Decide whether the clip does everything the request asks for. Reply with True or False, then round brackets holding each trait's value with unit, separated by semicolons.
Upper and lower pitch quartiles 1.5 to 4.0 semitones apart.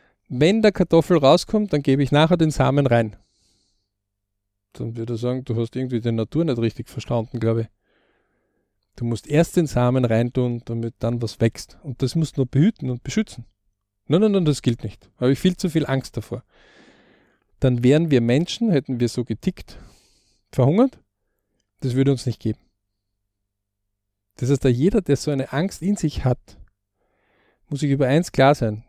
False (4.8 semitones)